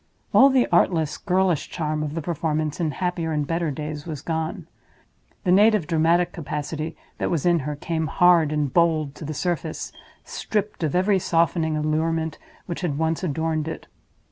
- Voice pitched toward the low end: No, medium, 160 Hz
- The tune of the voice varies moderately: No, narrow, 2.3 semitones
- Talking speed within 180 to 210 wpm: No, average, 170 wpm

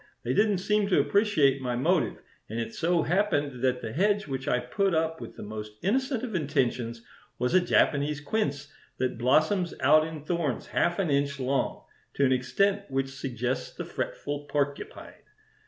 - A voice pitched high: No, medium, 145 Hz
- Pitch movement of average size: No, wide, 5.8 semitones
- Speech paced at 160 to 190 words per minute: Yes, average, 170 wpm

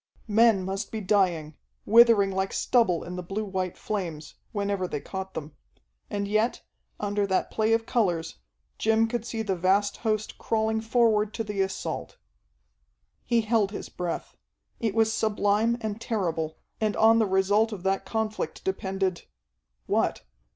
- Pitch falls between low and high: No, high, 205 Hz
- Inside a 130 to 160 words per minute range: Yes, average, 150 wpm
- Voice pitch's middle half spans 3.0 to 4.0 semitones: No, narrow, 2.6 semitones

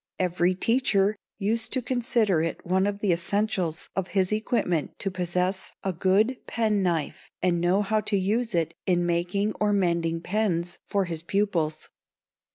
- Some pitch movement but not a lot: Yes, average, 3.4 semitones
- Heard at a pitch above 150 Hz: Yes, high, 190 Hz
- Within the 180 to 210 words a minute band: No, average, 155 wpm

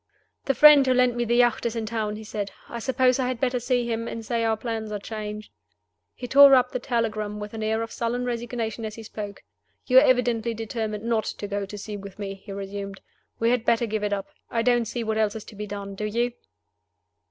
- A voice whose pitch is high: Yes, high, 225 Hz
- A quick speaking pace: Yes, fast, 240 wpm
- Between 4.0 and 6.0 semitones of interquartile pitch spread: No, narrow, 2.4 semitones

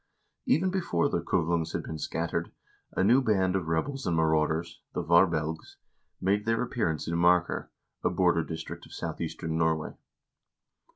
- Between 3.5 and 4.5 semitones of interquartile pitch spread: Yes, average, 4.2 semitones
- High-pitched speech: No, very low, 85 Hz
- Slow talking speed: No, average, 150 wpm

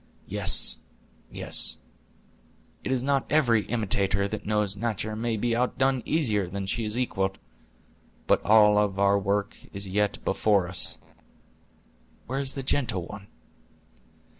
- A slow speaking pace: Yes, slow, 130 wpm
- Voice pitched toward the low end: Yes, low, 105 Hz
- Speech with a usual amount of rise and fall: Yes, average, 3.4 semitones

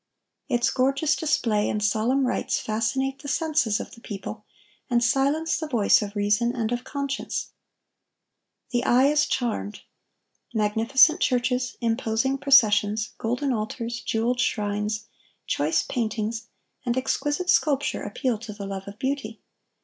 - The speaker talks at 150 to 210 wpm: No, slow, 135 wpm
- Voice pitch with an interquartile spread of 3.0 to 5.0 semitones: Yes, average, 4.0 semitones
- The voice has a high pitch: Yes, high, 235 Hz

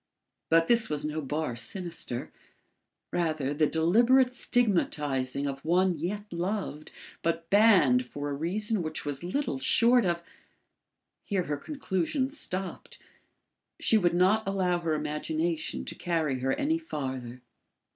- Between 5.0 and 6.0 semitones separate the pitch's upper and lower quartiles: Yes, wide, 5.4 semitones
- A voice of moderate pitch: Yes, medium, 170 Hz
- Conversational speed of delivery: No, slow, 130 wpm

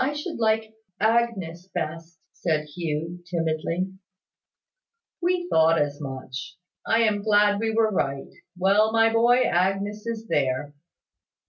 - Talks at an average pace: No, slow, 125 wpm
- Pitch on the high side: Yes, high, 195 Hz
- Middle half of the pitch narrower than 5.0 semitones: No, wide, 5.6 semitones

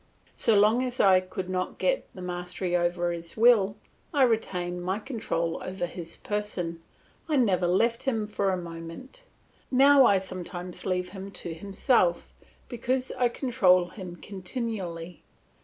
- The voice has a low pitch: No, high, 190 Hz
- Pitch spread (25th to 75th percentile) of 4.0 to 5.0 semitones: Yes, average, 4.7 semitones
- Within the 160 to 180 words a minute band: No, average, 145 wpm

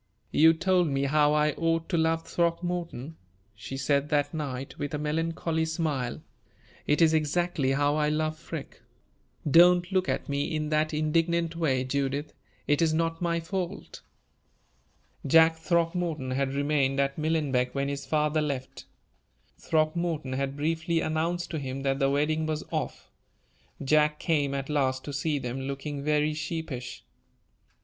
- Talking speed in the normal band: Yes, average, 150 wpm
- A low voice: No, medium, 150 Hz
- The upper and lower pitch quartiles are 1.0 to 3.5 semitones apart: Yes, average, 2.8 semitones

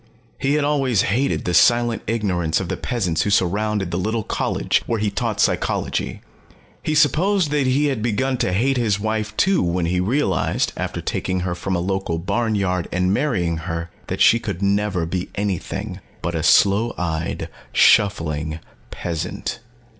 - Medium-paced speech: Yes, average, 165 wpm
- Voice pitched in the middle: No, low, 100 Hz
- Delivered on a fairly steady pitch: No, average, 5.1 semitones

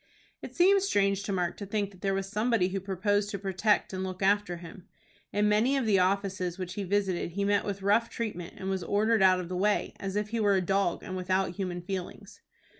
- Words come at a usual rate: No, fast, 230 wpm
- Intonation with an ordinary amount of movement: No, narrow, 1.9 semitones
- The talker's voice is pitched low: No, high, 195 Hz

